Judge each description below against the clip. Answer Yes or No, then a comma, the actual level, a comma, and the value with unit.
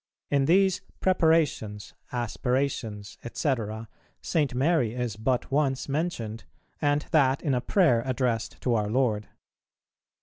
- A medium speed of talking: No, slow, 115 wpm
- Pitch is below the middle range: Yes, low, 130 Hz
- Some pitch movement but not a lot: Yes, average, 4.4 semitones